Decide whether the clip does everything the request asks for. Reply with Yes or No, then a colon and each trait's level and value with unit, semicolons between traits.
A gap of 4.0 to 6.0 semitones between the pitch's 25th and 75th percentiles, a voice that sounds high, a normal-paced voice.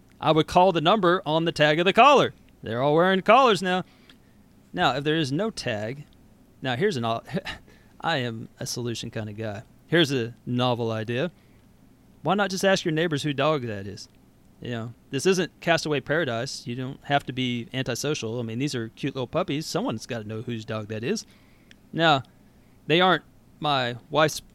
No: average, 5.3 semitones; low, 135 Hz; average, 190 wpm